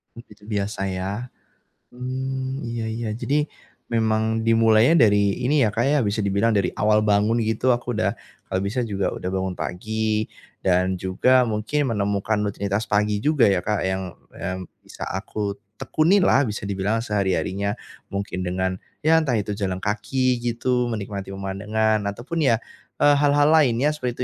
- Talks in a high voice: No, low, 110 Hz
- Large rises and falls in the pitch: No, average, 3.7 semitones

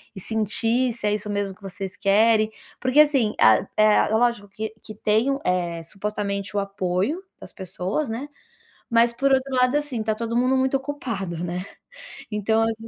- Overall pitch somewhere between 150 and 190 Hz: No, high, 215 Hz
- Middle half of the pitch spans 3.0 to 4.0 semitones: Yes, average, 3.7 semitones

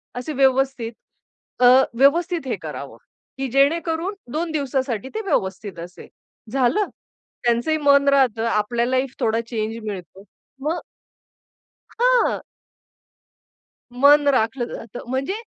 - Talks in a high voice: Yes, very high, 265 Hz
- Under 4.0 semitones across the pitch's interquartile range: No, average, 4.3 semitones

